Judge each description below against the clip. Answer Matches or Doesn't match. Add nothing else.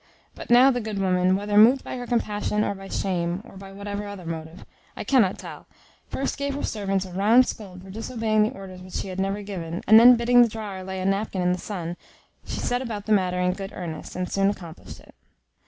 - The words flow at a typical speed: Doesn't match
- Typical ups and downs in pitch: Matches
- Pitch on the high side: Matches